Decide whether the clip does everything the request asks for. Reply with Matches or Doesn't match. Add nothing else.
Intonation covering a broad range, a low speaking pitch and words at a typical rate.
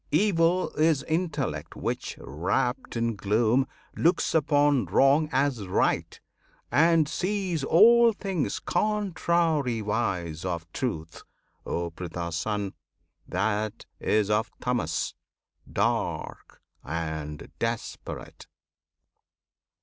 Doesn't match